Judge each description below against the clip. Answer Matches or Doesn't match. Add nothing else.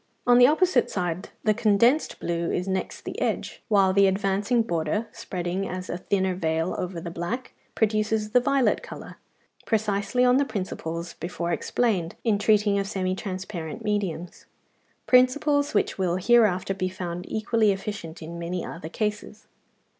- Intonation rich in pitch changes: Doesn't match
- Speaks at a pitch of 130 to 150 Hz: Doesn't match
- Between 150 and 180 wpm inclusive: Matches